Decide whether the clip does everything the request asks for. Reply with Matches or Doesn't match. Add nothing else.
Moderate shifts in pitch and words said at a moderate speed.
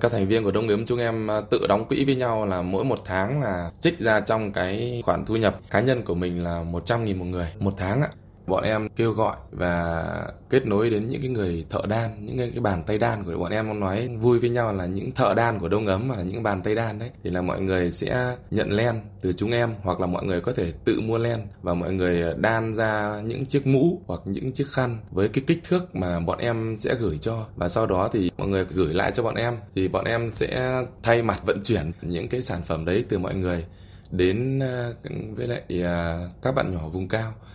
Matches